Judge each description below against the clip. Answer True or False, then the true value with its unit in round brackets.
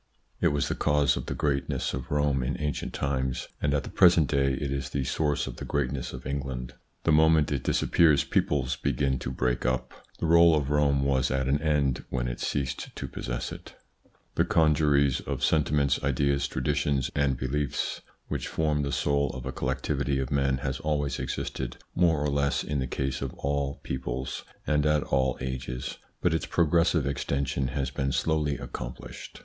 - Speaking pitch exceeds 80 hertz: False (70 Hz)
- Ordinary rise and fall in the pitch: False (2.1 semitones)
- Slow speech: False (185 wpm)